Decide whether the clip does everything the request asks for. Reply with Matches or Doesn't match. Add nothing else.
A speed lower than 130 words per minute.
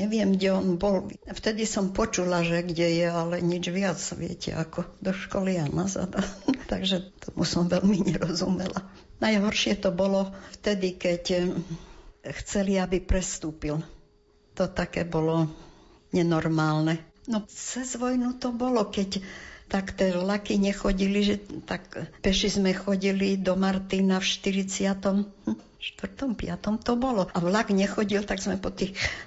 Doesn't match